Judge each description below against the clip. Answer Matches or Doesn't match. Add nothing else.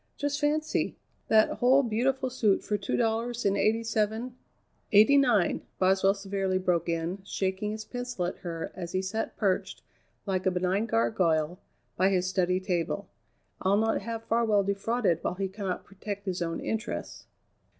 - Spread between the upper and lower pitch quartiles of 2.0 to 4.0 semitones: Matches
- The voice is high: Matches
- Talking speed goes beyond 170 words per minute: Doesn't match